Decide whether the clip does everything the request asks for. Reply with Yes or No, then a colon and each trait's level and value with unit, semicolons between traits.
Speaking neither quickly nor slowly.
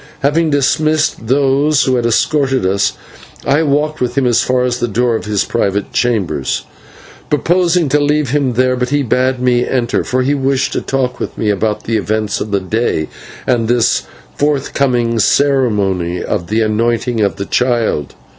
Yes: average, 175 wpm